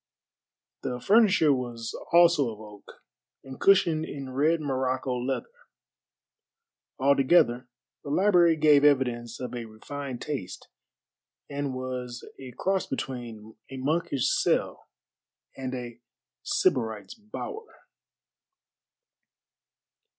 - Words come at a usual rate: No, slow, 100 wpm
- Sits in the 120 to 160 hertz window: Yes, low, 135 Hz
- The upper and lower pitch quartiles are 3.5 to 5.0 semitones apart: Yes, average, 4.1 semitones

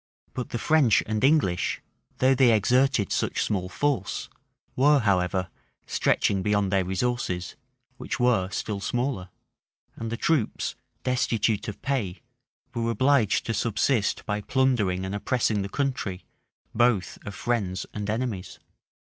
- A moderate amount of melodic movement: Yes, average, 4.5 semitones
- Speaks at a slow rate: Yes, slow, 130 wpm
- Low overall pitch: Yes, low, 110 Hz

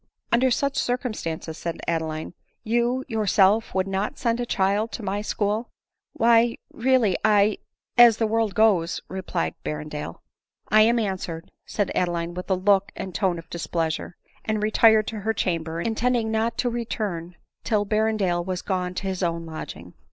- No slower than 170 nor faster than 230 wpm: Yes, average, 190 wpm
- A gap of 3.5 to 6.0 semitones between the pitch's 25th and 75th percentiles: Yes, average, 4.3 semitones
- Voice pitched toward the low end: No, high, 205 Hz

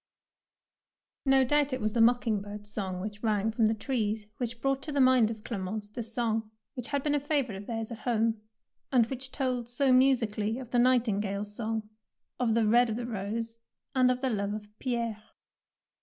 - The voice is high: Yes, high, 230 Hz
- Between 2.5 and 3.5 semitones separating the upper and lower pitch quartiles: Yes, average, 3.0 semitones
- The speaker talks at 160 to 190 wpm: No, fast, 205 wpm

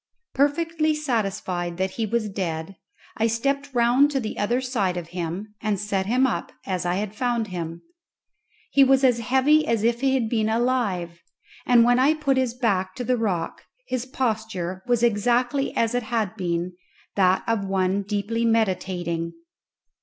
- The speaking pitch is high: Yes, high, 225 Hz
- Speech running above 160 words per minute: Yes, average, 170 wpm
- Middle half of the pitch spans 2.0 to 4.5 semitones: No, average, 5.0 semitones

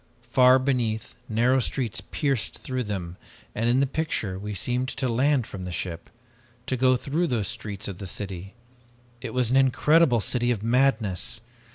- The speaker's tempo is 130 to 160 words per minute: No, average, 170 wpm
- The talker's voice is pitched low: Yes, low, 120 Hz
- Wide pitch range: No, average, 4.2 semitones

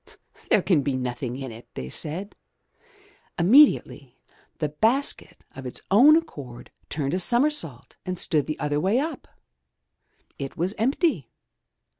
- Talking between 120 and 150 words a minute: Yes, slow, 135 wpm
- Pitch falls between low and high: Yes, medium, 160 Hz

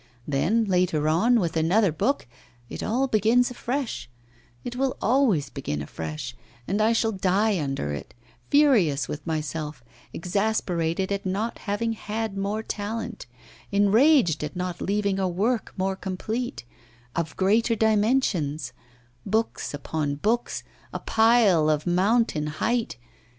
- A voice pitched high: Yes, high, 200 Hz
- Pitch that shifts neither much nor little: No, wide, 5.9 semitones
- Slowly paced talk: Yes, slow, 130 wpm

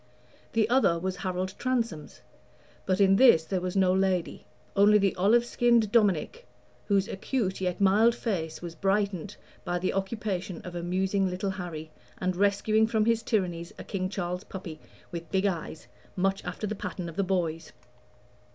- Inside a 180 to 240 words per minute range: No, average, 160 wpm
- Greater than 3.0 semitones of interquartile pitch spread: No, average, 2.7 semitones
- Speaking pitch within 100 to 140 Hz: No, high, 190 Hz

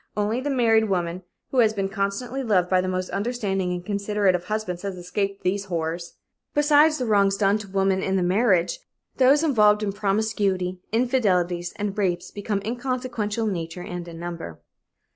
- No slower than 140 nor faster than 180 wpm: Yes, average, 170 wpm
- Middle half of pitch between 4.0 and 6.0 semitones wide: No, average, 3.4 semitones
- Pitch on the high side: Yes, high, 200 Hz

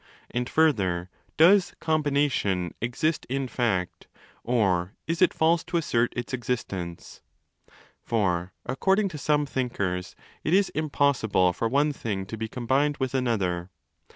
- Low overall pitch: Yes, low, 125 Hz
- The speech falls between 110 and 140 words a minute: Yes, slow, 135 wpm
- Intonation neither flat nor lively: No, wide, 7.5 semitones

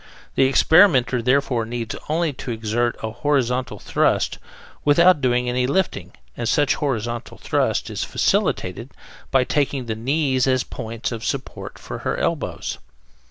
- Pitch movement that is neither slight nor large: Yes, average, 3.2 semitones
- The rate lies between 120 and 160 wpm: Yes, average, 140 wpm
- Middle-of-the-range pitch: No, low, 125 Hz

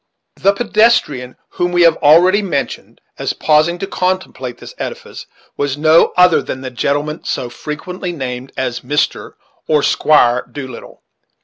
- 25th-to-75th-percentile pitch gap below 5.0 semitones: No, average, 5.3 semitones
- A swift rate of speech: No, average, 140 wpm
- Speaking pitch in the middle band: Yes, medium, 150 Hz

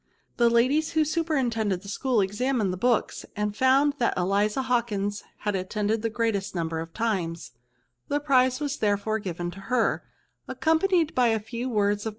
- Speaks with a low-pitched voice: No, high, 225 Hz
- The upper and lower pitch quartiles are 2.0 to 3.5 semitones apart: No, average, 4.3 semitones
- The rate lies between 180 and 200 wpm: No, average, 165 wpm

